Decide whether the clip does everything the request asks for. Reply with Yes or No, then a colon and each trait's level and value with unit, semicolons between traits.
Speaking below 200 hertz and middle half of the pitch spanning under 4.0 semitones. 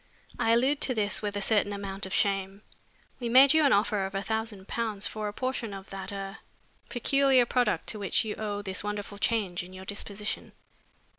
No: high, 210 Hz; average, 2.9 semitones